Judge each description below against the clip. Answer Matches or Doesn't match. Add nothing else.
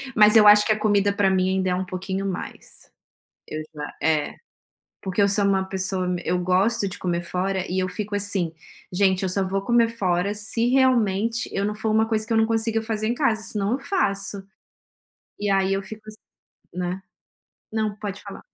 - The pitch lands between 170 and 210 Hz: Matches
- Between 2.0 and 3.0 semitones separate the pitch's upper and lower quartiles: Matches